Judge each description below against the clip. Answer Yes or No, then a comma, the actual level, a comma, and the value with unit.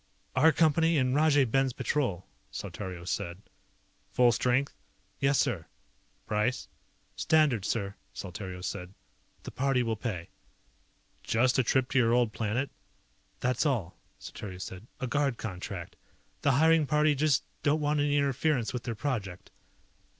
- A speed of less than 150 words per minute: Yes, slow, 135 wpm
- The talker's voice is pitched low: Yes, low, 125 Hz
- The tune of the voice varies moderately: No, wide, 5.7 semitones